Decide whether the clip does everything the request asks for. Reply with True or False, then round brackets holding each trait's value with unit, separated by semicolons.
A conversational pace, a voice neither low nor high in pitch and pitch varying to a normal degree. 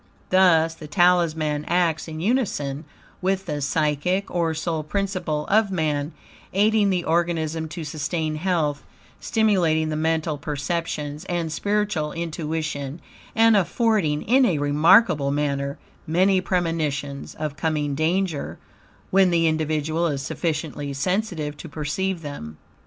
False (125 wpm; 160 Hz; 3.4 semitones)